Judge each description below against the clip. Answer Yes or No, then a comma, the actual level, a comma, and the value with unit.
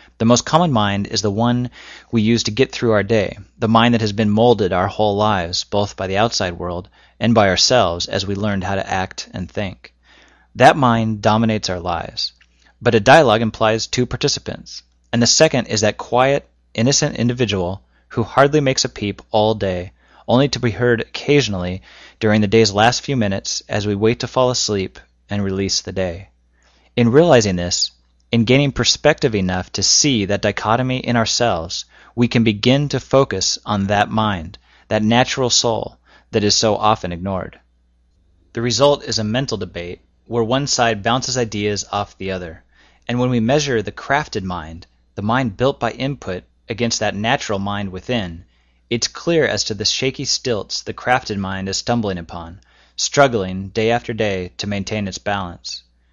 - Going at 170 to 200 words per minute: Yes, average, 180 wpm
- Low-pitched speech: Yes, low, 110 Hz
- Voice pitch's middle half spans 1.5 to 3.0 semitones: No, average, 4.0 semitones